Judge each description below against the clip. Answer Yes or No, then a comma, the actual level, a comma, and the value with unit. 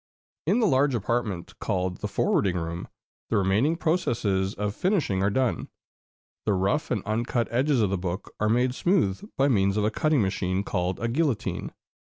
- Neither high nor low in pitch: No, low, 110 Hz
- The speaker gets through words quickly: No, average, 175 wpm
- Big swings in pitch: Yes, wide, 5.7 semitones